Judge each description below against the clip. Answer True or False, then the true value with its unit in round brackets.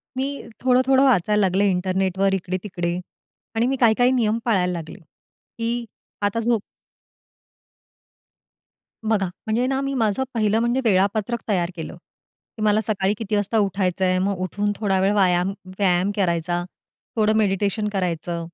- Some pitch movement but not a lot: True (3.6 semitones)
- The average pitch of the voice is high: True (205 Hz)